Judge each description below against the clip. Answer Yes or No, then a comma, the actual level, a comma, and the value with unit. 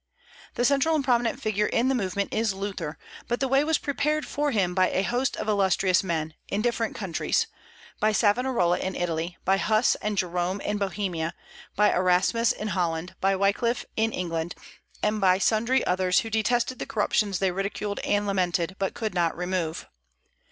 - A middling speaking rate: Yes, average, 175 wpm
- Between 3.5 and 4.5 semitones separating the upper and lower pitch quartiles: Yes, average, 4.1 semitones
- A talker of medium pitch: No, high, 200 Hz